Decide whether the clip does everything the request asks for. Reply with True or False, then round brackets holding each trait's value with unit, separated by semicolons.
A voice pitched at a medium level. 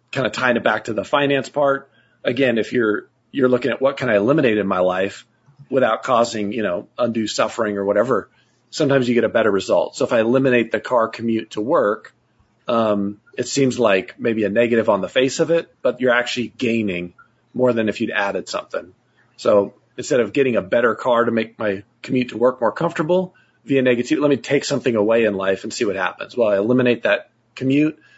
False (120 Hz)